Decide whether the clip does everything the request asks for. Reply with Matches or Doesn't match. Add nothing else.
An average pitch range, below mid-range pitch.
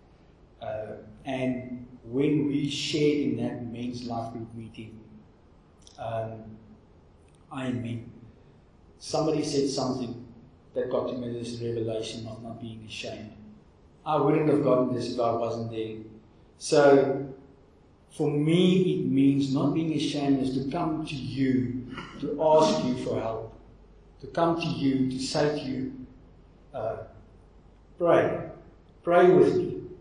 Matches